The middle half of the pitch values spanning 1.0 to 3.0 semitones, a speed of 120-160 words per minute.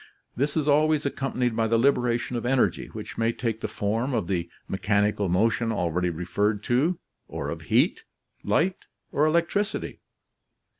No: wide, 5.4 semitones; average, 150 wpm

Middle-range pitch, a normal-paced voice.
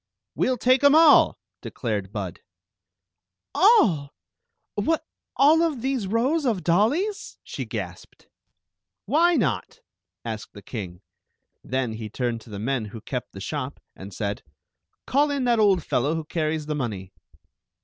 Yes: medium, 155 Hz; average, 160 wpm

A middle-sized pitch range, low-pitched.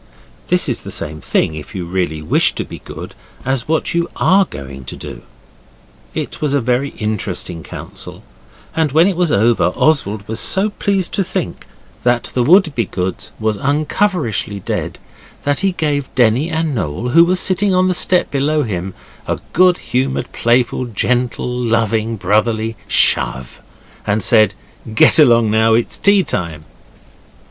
No: wide, 7.1 semitones; low, 120 Hz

